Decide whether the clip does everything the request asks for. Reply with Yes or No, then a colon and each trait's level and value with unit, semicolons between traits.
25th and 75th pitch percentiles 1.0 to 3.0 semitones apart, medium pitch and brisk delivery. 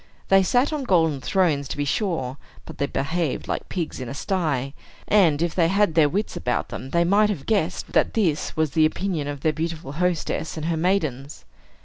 No: average, 4.5 semitones; medium, 160 Hz; fast, 210 wpm